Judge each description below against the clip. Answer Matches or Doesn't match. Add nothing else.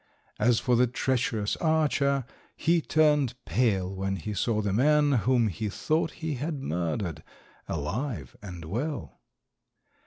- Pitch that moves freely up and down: Matches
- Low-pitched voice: Matches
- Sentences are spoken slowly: Matches